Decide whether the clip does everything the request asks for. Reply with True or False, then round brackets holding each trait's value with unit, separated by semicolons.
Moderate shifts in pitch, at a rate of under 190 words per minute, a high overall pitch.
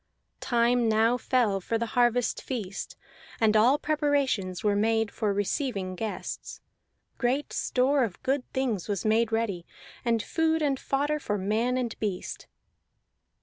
True (3.8 semitones; 140 wpm; 230 Hz)